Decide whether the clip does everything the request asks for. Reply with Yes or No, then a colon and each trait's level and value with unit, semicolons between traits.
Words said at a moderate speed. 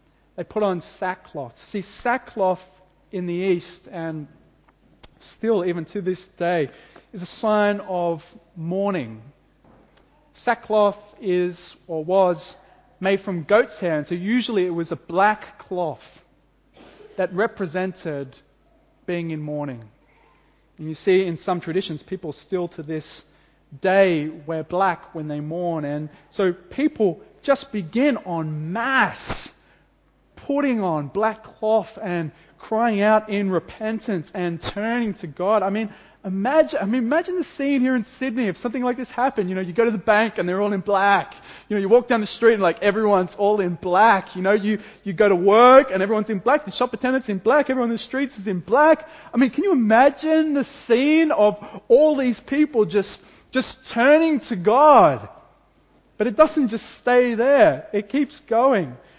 Yes: average, 170 wpm